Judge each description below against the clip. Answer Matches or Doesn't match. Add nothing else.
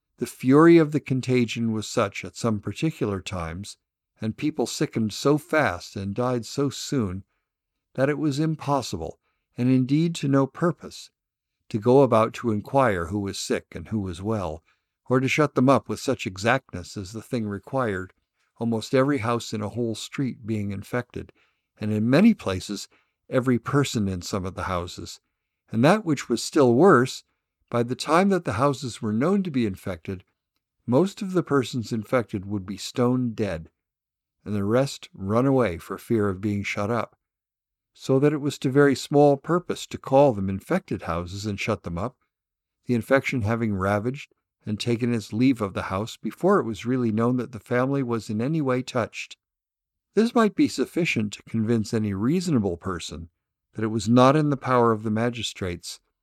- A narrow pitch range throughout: Doesn't match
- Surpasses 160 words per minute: Matches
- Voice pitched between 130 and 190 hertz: Doesn't match